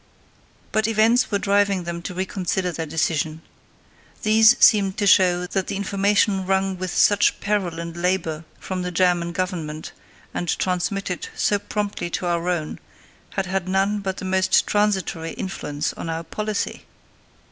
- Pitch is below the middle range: No, medium, 185 Hz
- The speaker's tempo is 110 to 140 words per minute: No, average, 150 wpm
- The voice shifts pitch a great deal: No, average, 2.7 semitones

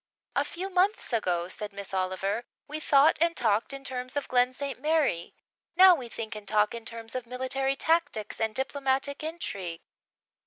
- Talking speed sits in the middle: Yes, average, 170 wpm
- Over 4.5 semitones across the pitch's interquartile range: Yes, average, 5.2 semitones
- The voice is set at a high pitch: Yes, very high, 255 Hz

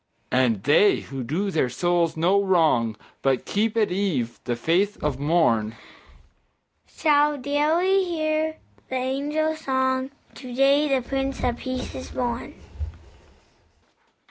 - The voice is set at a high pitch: Yes, high, 235 Hz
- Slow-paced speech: Yes, slow, 125 wpm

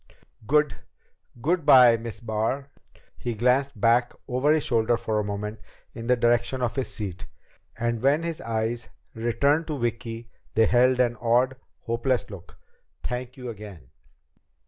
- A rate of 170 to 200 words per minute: No, average, 145 wpm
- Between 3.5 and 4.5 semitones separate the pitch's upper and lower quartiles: No, narrow, 2.5 semitones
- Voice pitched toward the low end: Yes, low, 120 Hz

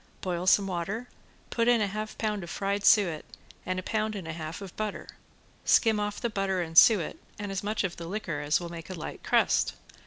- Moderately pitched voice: No, high, 195 Hz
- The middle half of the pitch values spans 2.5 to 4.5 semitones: Yes, average, 3.7 semitones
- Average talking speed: No, fast, 220 wpm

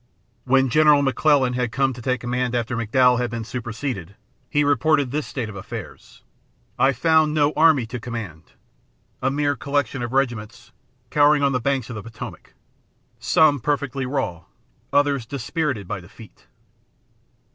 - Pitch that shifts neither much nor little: Yes, average, 3.6 semitones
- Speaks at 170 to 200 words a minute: No, average, 145 wpm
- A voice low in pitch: Yes, low, 130 Hz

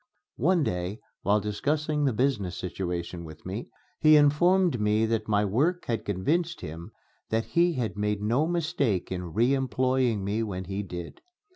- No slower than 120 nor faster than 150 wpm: No, average, 160 wpm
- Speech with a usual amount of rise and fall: No, wide, 7.1 semitones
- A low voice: Yes, low, 110 Hz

